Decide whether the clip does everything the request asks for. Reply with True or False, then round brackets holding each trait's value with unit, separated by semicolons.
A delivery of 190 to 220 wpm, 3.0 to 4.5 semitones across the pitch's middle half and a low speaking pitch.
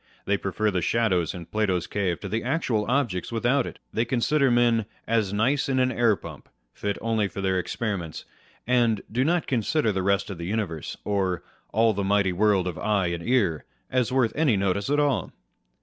True (200 wpm; 4.1 semitones; 110 Hz)